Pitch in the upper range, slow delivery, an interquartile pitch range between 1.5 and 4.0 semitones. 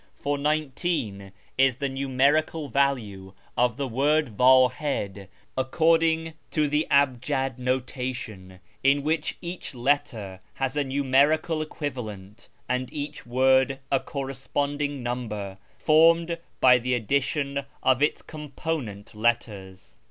No: low, 135 Hz; slow, 110 wpm; average, 3.5 semitones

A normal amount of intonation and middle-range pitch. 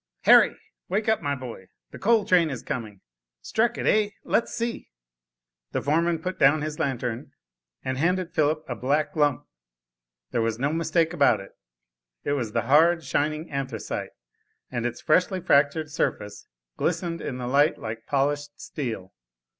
Yes: average, 4.6 semitones; medium, 145 Hz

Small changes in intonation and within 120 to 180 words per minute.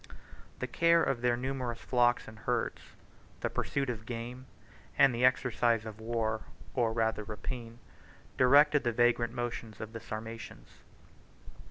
Yes: narrow, 1.9 semitones; average, 150 wpm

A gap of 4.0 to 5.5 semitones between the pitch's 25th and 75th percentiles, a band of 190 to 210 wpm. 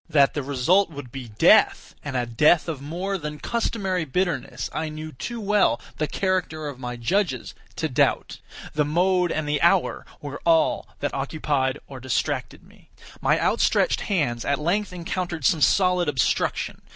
No: average, 4.8 semitones; average, 165 wpm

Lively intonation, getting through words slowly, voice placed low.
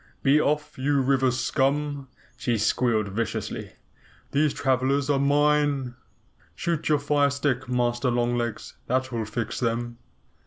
No: average, 3.1 semitones; slow, 130 wpm; low, 130 Hz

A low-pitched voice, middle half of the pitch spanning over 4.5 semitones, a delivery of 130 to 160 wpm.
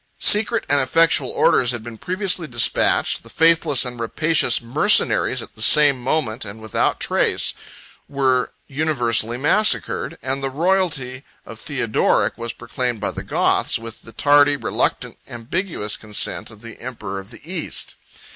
Yes: low, 130 Hz; average, 5.1 semitones; average, 145 wpm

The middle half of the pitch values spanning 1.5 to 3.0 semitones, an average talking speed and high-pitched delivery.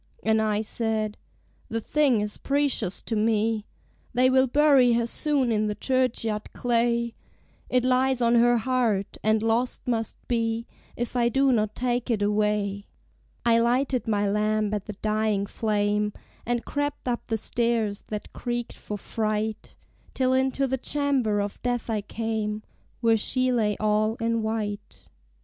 Yes: narrow, 2.6 semitones; average, 155 wpm; high, 225 Hz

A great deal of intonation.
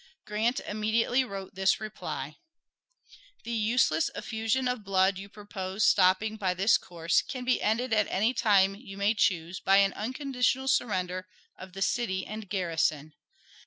No: average, 3.2 semitones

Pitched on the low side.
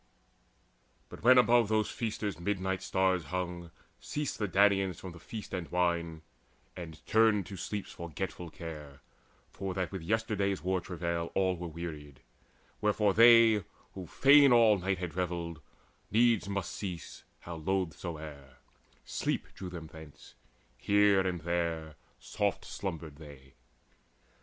Yes: very low, 90 Hz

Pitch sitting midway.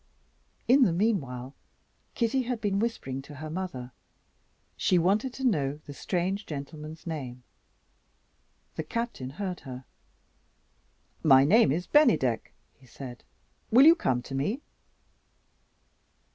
Yes: medium, 160 Hz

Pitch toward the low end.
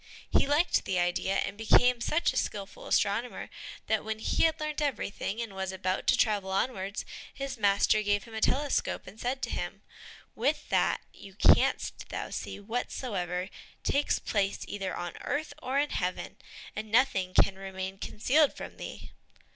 No: high, 210 Hz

